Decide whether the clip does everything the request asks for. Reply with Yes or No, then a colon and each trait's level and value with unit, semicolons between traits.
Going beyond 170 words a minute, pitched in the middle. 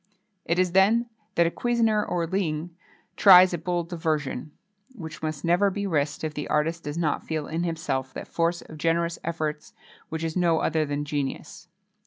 Yes: average, 180 wpm; medium, 165 Hz